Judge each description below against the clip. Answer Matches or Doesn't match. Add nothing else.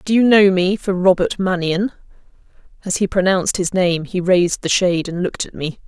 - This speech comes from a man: Doesn't match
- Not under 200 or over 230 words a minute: Matches